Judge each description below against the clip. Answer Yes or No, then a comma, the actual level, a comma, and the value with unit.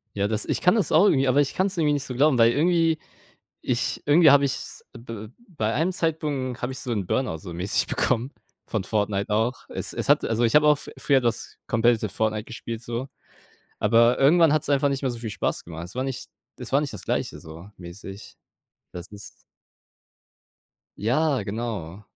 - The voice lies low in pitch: Yes, low, 120 Hz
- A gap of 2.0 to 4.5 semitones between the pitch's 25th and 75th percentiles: No, average, 5.1 semitones